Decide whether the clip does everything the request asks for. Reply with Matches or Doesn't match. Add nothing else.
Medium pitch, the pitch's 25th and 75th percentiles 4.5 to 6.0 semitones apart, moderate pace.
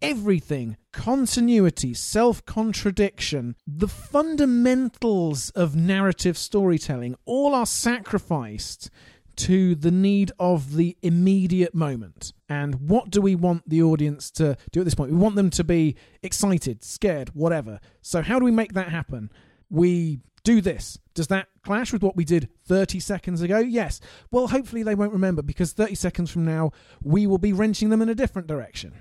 Matches